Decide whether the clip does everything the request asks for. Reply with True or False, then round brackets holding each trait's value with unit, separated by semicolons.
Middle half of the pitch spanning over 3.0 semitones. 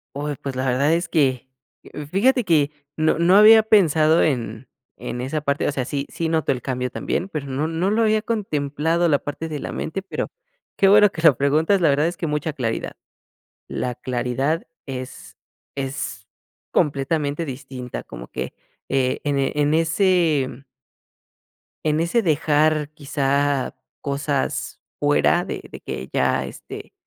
True (3.5 semitones)